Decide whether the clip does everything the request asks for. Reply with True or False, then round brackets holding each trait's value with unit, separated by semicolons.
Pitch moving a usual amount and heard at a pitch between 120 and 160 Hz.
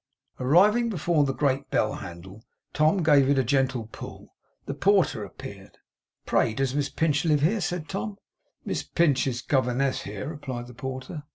True (3.9 semitones; 140 Hz)